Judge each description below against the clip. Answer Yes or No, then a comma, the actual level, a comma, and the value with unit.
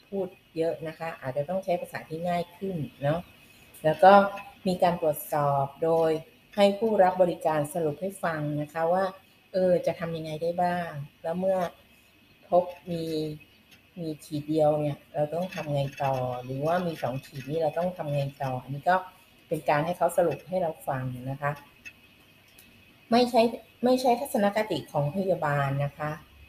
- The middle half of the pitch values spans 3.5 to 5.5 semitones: Yes, average, 3.9 semitones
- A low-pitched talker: No, medium, 165 Hz